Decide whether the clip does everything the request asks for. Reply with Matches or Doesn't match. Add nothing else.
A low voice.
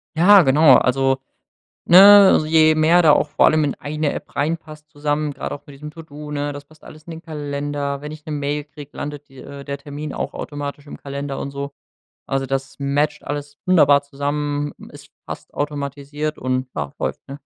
Doesn't match